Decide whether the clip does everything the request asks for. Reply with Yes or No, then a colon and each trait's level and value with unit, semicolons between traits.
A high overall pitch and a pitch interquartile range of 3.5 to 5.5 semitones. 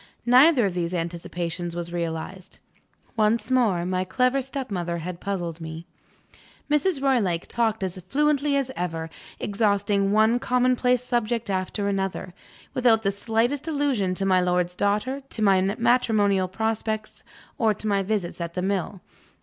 Yes: high, 200 Hz; average, 5.0 semitones